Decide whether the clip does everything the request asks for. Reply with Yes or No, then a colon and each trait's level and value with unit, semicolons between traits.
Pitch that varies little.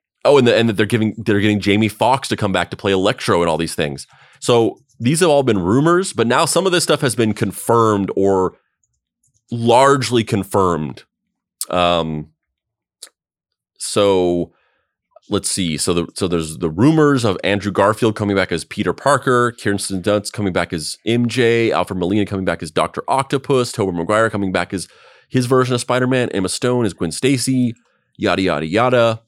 No: average, 4.3 semitones